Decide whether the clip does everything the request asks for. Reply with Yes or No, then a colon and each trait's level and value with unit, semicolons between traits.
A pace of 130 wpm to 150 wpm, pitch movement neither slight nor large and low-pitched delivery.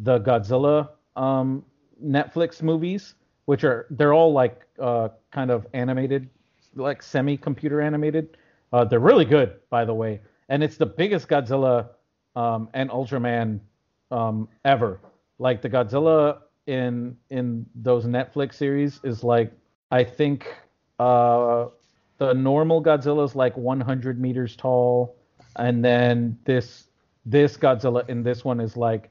Yes: average, 140 wpm; average, 3.1 semitones; low, 130 Hz